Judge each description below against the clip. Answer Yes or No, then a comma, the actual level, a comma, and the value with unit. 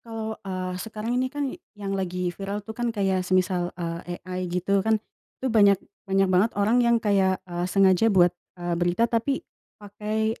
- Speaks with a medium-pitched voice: No, high, 195 Hz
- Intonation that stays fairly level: No, average, 3.3 semitones